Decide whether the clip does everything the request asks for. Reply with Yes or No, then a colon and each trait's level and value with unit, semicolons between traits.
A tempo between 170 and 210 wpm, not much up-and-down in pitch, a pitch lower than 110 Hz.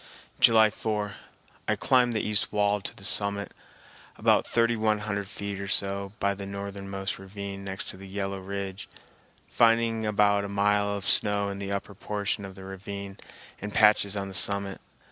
Yes: average, 175 wpm; narrow, 1.0 semitones; low, 100 Hz